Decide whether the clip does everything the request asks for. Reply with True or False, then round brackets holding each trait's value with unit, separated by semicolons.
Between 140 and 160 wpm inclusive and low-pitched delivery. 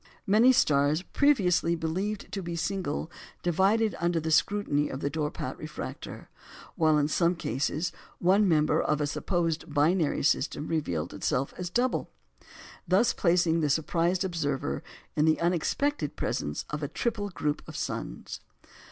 False (145 wpm; 170 Hz)